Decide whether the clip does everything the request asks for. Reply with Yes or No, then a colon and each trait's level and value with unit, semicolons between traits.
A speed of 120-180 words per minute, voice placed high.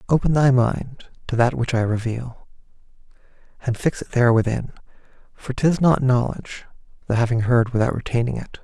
No: average, 160 wpm; low, 125 Hz